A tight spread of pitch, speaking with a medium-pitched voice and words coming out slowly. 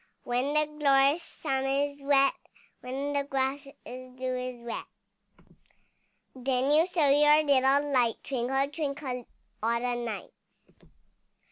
No: narrow, 2.2 semitones; very high, 275 Hz; slow, 125 wpm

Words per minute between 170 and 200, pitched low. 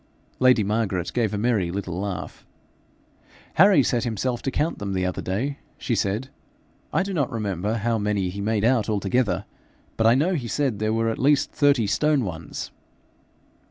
Yes: average, 175 wpm; low, 115 Hz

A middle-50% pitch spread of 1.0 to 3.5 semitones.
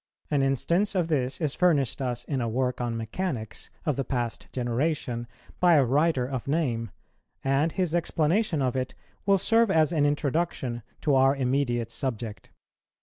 No: average, 4.6 semitones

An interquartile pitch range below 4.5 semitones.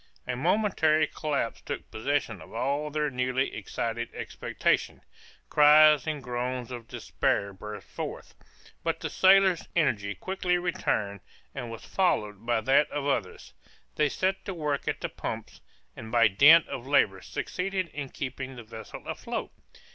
No: average, 5.1 semitones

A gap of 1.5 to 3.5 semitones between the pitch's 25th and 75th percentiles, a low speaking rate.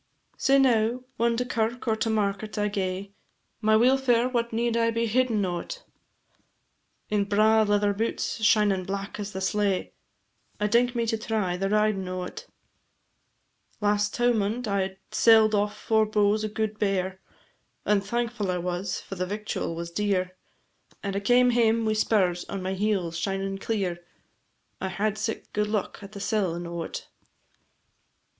No: narrow, 2.5 semitones; average, 155 wpm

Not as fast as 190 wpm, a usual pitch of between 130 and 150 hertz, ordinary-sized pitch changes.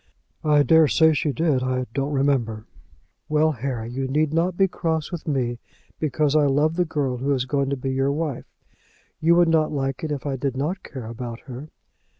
No: average, 195 wpm; medium, 140 Hz; average, 3.1 semitones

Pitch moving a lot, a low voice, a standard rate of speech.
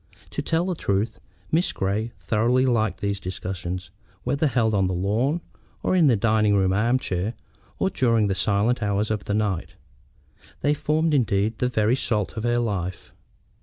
No: average, 4.0 semitones; low, 110 Hz; average, 170 wpm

